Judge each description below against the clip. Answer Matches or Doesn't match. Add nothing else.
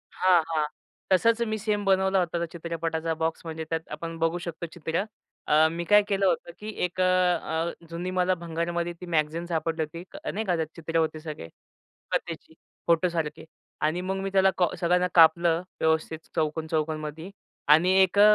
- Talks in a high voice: Doesn't match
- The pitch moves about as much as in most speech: Doesn't match